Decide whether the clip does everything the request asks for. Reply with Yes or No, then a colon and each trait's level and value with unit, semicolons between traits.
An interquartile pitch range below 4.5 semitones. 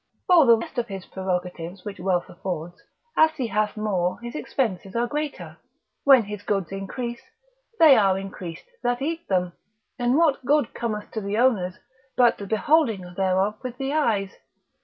No: average, 5.0 semitones